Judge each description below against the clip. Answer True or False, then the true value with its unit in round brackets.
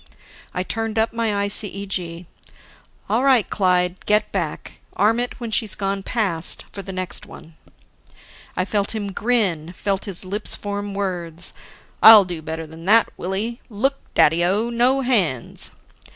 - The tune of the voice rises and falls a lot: False (3.7 semitones)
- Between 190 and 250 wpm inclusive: False (150 wpm)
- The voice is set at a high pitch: True (200 Hz)